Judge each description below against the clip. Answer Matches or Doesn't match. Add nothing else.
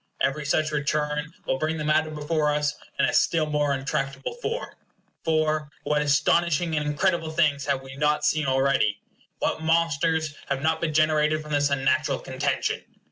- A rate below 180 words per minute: Matches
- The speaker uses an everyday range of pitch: Doesn't match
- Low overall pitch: Doesn't match